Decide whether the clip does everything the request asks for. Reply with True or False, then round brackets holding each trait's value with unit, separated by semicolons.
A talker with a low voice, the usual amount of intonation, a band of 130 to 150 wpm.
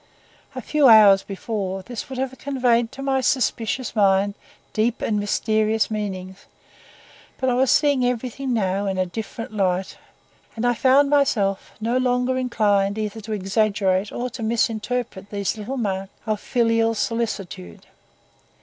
False (220 Hz; 3.8 semitones; 145 wpm)